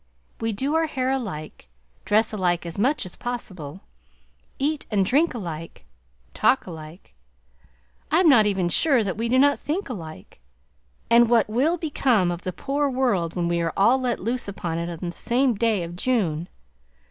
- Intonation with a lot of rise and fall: Yes, wide, 6.9 semitones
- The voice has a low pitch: No, high, 215 Hz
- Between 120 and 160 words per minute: No, average, 175 wpm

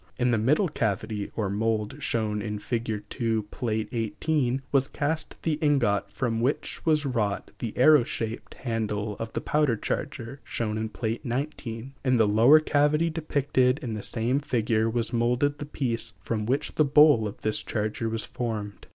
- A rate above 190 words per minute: No, average, 170 wpm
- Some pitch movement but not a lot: Yes, average, 4.4 semitones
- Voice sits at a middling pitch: No, low, 120 Hz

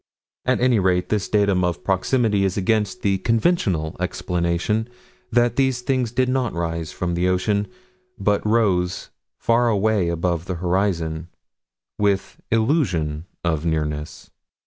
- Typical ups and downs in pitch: Yes, average, 4.6 semitones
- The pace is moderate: No, slow, 130 wpm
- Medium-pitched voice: No, very low, 95 Hz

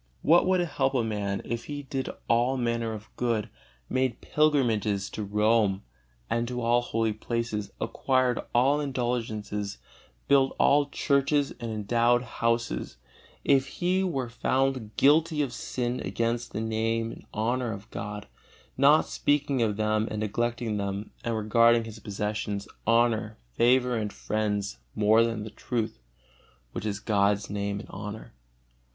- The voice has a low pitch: Yes, low, 115 Hz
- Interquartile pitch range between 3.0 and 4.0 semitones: Yes, average, 3.3 semitones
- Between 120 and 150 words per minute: Yes, average, 145 wpm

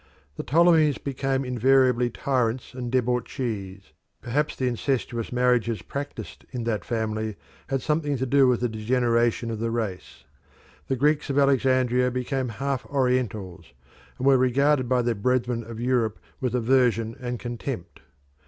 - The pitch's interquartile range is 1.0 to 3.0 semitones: Yes, narrow, 2.4 semitones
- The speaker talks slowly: No, average, 145 wpm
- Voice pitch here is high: No, low, 125 Hz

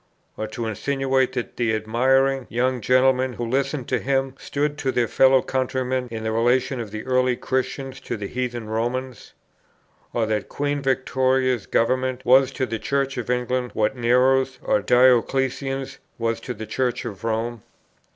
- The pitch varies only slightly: Yes, narrow, 2.1 semitones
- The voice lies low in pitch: Yes, low, 125 Hz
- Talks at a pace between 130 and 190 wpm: Yes, average, 160 wpm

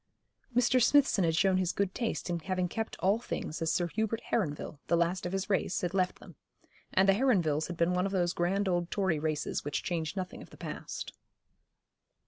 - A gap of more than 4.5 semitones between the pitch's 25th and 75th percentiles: No, average, 2.7 semitones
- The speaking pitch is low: No, medium, 185 Hz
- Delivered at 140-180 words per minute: No, fast, 205 wpm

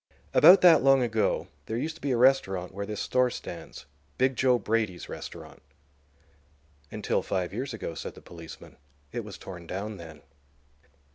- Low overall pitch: Yes, low, 110 Hz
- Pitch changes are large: Yes, wide, 6.1 semitones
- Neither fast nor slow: Yes, average, 155 wpm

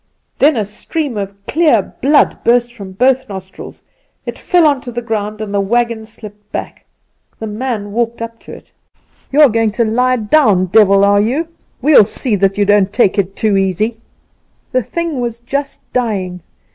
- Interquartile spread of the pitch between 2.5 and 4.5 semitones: Yes, average, 3.8 semitones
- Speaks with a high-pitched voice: Yes, high, 225 Hz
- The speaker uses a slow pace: No, average, 175 wpm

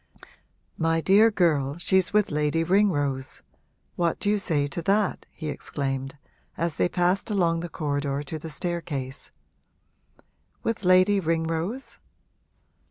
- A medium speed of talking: No, slow, 125 wpm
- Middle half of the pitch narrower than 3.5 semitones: No, average, 4.4 semitones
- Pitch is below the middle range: No, medium, 165 Hz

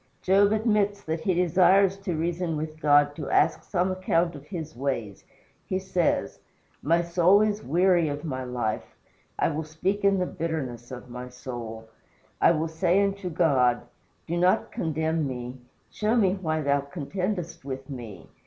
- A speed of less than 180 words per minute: Yes, average, 160 wpm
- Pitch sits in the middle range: Yes, medium, 160 Hz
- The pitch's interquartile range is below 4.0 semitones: No, average, 5.0 semitones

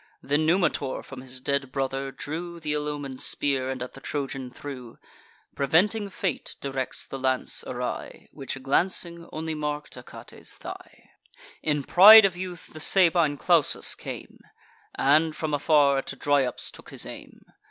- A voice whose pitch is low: No, medium, 145 Hz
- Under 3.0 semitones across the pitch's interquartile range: No, average, 3.6 semitones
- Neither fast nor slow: Yes, average, 150 wpm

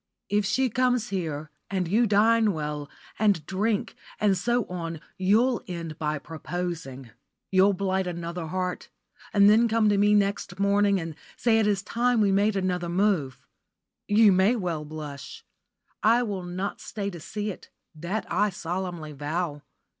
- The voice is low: No, high, 190 Hz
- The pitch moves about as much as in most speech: Yes, average, 3.8 semitones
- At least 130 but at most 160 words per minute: Yes, average, 155 wpm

